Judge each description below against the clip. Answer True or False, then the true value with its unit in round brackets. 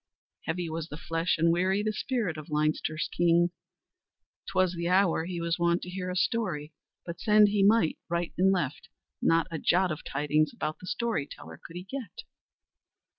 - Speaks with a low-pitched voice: False (175 Hz)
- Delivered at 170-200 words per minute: True (180 wpm)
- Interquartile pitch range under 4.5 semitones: True (2.8 semitones)